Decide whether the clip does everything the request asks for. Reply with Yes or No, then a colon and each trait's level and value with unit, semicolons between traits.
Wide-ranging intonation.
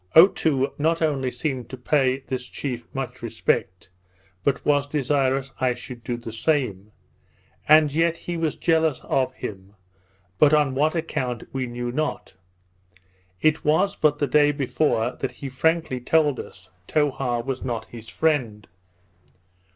No: average, 3.7 semitones